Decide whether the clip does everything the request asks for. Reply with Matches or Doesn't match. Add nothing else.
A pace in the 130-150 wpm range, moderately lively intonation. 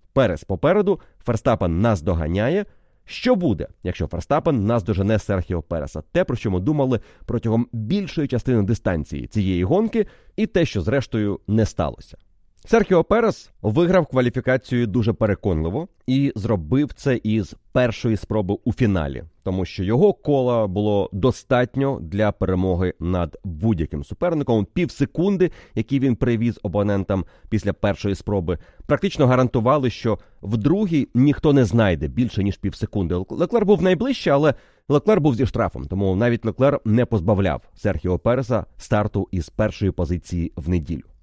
Doesn't match